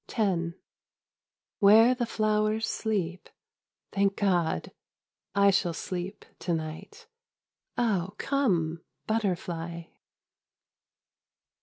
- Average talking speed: No, slow, 75 wpm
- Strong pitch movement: No, average, 4.1 semitones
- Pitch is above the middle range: Yes, high, 195 Hz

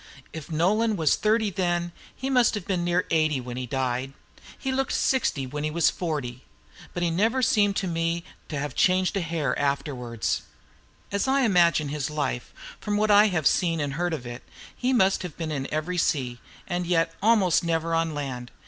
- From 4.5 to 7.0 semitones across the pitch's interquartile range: Yes, average, 5.1 semitones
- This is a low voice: No, medium, 165 Hz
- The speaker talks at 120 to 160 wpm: No, average, 190 wpm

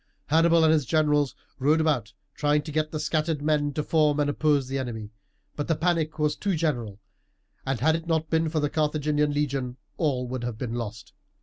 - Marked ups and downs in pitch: No, average, 2.8 semitones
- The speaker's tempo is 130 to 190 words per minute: No, average, 200 wpm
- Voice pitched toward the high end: No, medium, 150 Hz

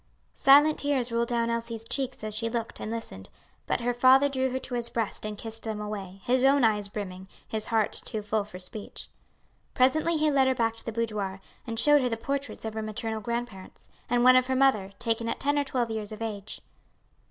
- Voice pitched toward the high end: Yes, high, 230 Hz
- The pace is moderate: No, fast, 220 wpm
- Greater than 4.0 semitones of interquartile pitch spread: No, average, 3.2 semitones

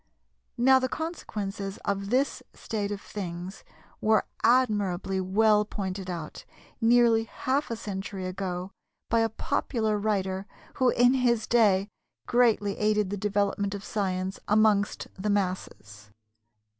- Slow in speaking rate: Yes, slow, 125 wpm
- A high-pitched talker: Yes, high, 205 Hz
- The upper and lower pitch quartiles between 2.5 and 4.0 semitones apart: Yes, average, 2.9 semitones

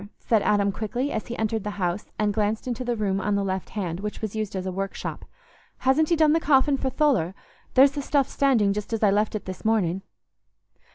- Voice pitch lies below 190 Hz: No, high, 215 Hz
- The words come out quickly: Yes, fast, 225 wpm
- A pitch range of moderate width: Yes, average, 4.7 semitones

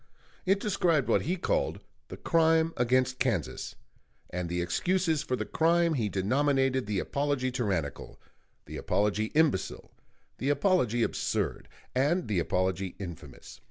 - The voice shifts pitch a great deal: Yes, wide, 8.1 semitones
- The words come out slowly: Yes, slow, 130 wpm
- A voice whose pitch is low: Yes, low, 130 Hz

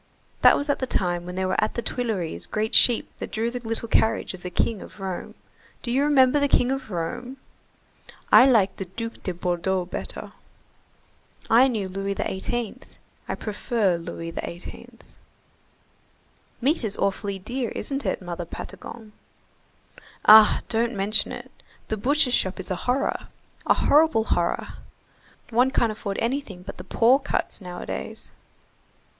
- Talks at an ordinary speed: Yes, average, 150 wpm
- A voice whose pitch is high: Yes, high, 220 Hz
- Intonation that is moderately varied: Yes, average, 4.8 semitones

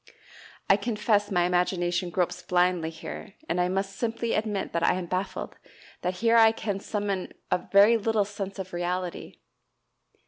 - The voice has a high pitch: Yes, high, 195 Hz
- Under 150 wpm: No, average, 160 wpm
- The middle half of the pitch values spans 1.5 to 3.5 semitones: Yes, average, 2.7 semitones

